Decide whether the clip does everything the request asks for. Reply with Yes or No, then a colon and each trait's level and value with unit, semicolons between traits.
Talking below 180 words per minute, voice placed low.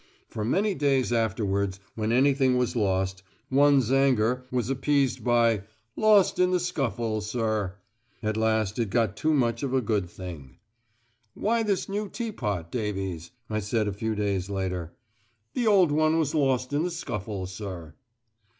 Yes: average, 155 wpm; low, 115 Hz